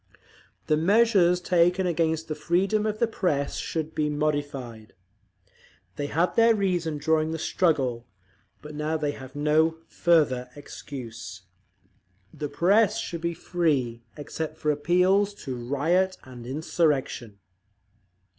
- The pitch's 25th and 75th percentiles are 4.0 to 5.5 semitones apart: No, average, 3.6 semitones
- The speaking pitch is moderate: Yes, medium, 155 Hz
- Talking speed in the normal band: No, slow, 125 wpm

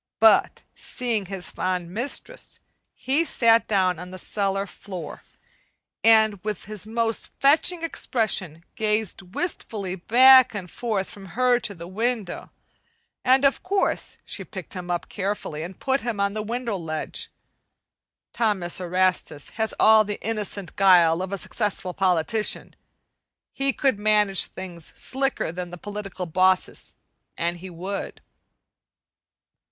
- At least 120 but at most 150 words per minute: Yes, slow, 135 wpm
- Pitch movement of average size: Yes, average, 3.9 semitones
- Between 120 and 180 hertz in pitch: No, high, 200 Hz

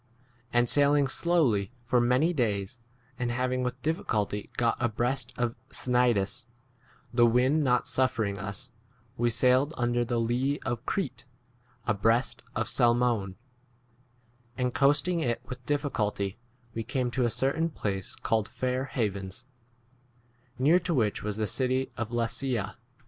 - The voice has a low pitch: Yes, low, 120 Hz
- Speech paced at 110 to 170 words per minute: Yes, average, 140 wpm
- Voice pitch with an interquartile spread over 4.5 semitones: No, average, 2.7 semitones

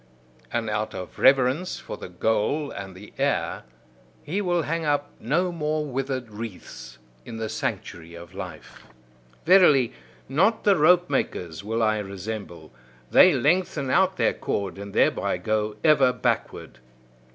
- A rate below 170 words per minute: Yes, average, 140 wpm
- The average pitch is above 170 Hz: No, low, 125 Hz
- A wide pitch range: Yes, wide, 7.0 semitones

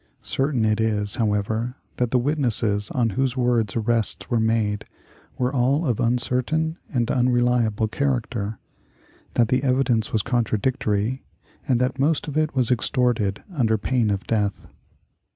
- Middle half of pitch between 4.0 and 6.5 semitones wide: No, average, 2.9 semitones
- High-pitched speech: No, low, 120 Hz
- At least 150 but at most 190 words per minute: No, average, 140 wpm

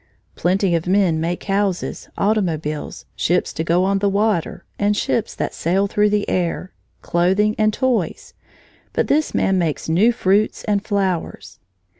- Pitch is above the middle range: Yes, high, 195 Hz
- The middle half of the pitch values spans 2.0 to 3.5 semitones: Yes, average, 3.1 semitones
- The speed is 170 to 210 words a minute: No, average, 150 wpm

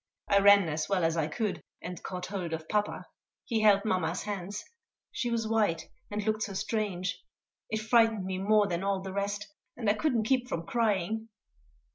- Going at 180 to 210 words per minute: Yes, average, 185 wpm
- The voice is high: Yes, high, 200 Hz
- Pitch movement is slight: No, average, 3.0 semitones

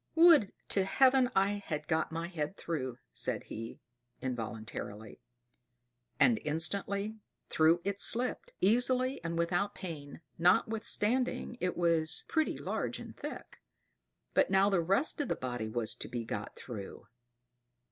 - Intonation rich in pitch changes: Yes, wide, 6.9 semitones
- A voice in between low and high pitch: Yes, medium, 175 Hz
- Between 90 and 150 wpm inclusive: Yes, slow, 135 wpm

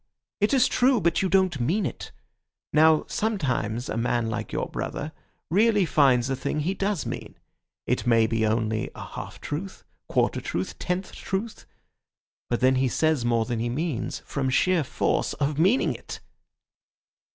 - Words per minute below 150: No, average, 160 wpm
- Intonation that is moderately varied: No, wide, 7.8 semitones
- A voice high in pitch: No, medium, 150 Hz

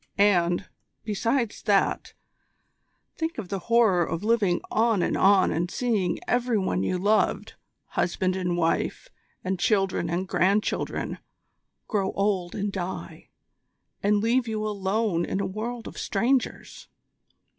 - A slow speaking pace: Yes, slow, 130 wpm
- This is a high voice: Yes, high, 200 Hz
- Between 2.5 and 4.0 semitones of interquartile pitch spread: Yes, average, 3.5 semitones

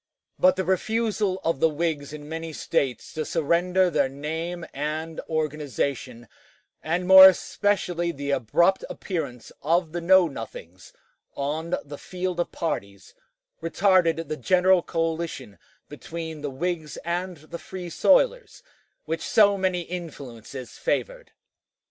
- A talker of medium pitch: Yes, medium, 165 Hz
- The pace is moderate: No, slow, 125 wpm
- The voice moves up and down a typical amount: Yes, average, 3.8 semitones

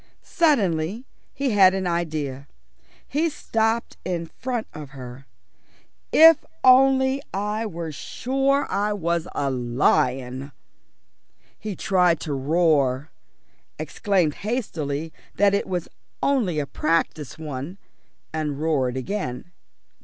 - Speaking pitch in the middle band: Yes, medium, 170 Hz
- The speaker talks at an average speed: No, slow, 110 wpm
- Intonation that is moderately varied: No, wide, 7.1 semitones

